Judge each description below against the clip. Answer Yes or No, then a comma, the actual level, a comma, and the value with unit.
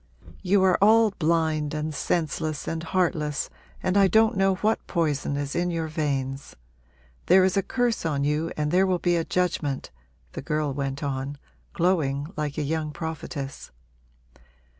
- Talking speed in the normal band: Yes, average, 160 wpm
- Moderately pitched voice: Yes, medium, 160 Hz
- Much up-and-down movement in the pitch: No, average, 3.8 semitones